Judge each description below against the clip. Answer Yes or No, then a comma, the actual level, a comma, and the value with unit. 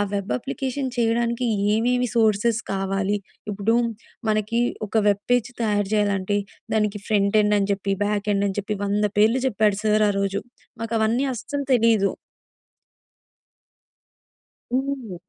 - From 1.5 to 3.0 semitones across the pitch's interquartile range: Yes, narrow, 2.6 semitones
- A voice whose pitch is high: Yes, high, 210 Hz